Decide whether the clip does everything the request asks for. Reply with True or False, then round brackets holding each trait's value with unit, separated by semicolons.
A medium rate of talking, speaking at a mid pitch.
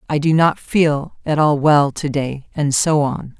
False (210 wpm; 150 Hz)